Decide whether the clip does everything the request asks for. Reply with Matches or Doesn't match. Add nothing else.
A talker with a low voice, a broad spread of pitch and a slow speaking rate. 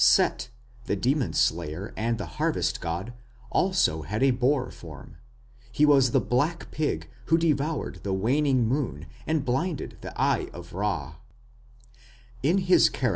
Matches